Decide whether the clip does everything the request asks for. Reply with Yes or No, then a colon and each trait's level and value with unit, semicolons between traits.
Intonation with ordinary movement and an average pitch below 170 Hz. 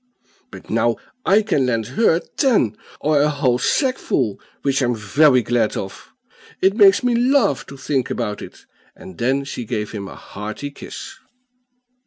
No: wide, 8.6 semitones; low, 135 Hz